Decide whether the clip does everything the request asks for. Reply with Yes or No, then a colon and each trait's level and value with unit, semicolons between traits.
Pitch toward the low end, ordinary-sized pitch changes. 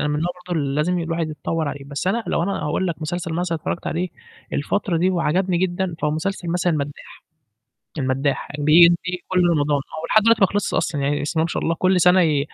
No: medium, 170 Hz; average, 3.3 semitones